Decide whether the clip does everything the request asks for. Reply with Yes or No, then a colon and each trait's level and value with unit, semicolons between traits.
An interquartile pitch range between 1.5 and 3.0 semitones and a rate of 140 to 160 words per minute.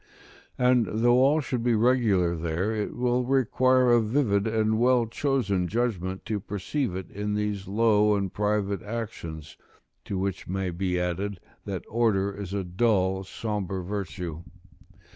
No: average, 3.8 semitones; average, 145 wpm